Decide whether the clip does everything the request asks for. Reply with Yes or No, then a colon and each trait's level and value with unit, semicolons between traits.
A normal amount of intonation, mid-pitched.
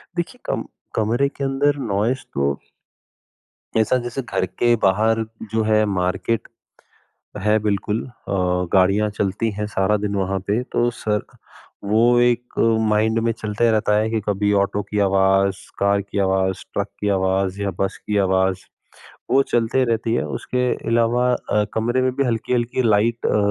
No: average, 3.2 semitones; low, 105 Hz